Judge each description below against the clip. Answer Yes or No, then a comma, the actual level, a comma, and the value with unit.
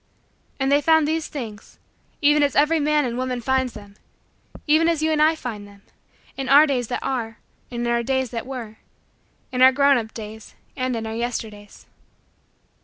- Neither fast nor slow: Yes, average, 185 wpm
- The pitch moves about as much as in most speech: Yes, average, 4.2 semitones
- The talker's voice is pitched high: Yes, very high, 255 Hz